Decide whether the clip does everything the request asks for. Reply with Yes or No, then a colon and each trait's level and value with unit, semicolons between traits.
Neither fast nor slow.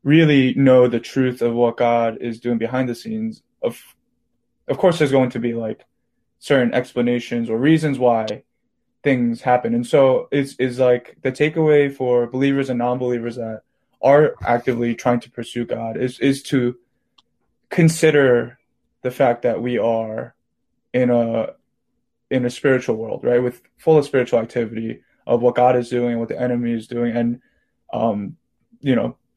Yes: average, 165 wpm